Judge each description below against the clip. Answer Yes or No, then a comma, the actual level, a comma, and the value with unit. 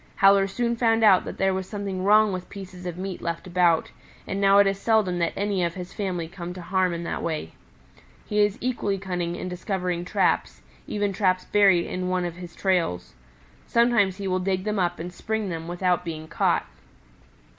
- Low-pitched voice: No, medium, 185 Hz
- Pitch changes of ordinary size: No, narrow, 2.2 semitones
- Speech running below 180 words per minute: No, average, 200 wpm